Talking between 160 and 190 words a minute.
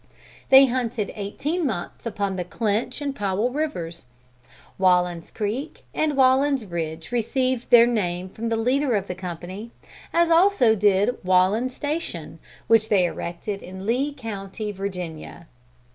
No: slow, 135 wpm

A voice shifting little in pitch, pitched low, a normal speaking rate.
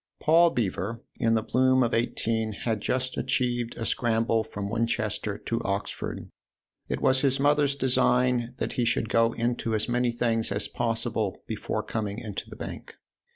Yes: narrow, 2.2 semitones; low, 115 Hz; average, 165 wpm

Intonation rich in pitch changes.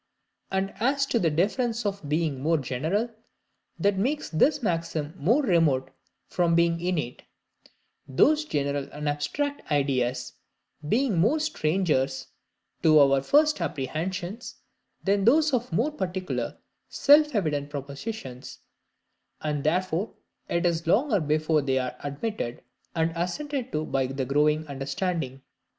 Yes: wide, 7.2 semitones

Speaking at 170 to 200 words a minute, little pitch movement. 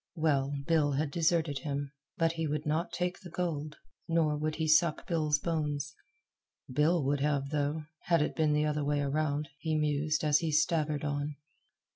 Yes: average, 175 wpm; narrow, 1.8 semitones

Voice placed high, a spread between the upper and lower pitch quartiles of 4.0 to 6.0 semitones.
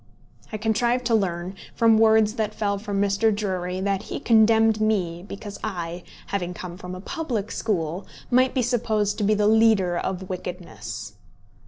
No: high, 205 Hz; average, 3.1 semitones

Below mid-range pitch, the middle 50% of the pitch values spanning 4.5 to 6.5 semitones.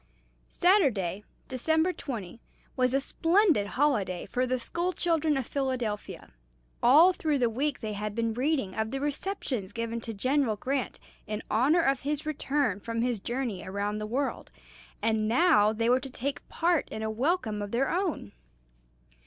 No: very high, 255 Hz; average, 5.2 semitones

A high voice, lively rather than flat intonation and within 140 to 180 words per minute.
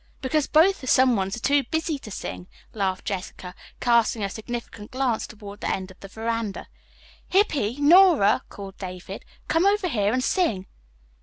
Yes: high, 230 Hz; wide, 6.5 semitones; average, 160 wpm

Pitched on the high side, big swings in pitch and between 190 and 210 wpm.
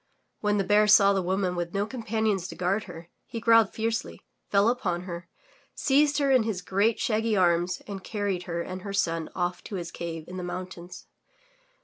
No: high, 195 Hz; average, 3.5 semitones; average, 195 wpm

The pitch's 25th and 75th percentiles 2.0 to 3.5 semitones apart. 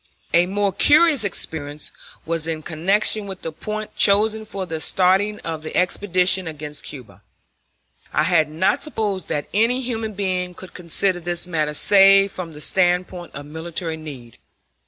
No: average, 4.0 semitones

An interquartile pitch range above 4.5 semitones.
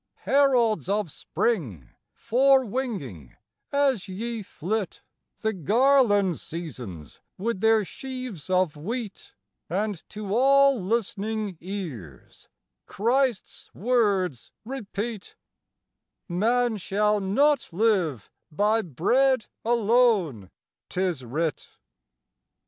Yes: average, 5.2 semitones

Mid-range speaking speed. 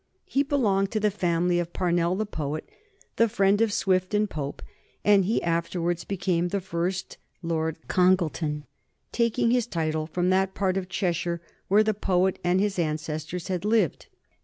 Yes: average, 160 wpm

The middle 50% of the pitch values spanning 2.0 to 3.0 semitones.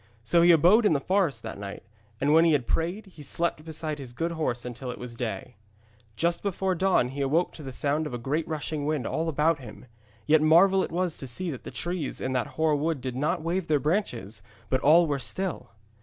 No: average, 4.4 semitones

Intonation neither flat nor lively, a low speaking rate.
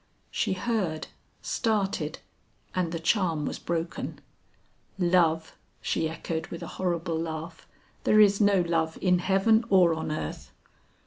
Yes: average, 3.0 semitones; slow, 130 wpm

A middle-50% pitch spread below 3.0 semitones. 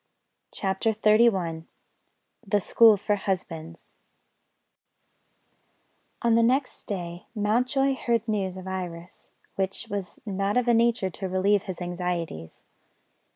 No: average, 3.9 semitones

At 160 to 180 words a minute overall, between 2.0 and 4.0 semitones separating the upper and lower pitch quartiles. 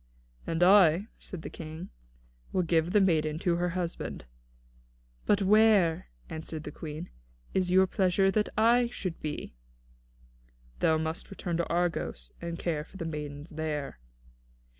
No: average, 145 wpm; average, 3.1 semitones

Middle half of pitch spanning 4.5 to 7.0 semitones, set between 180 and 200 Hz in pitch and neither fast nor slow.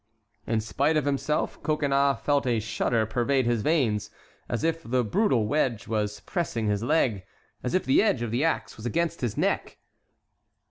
No: average, 5.1 semitones; low, 125 Hz; average, 170 wpm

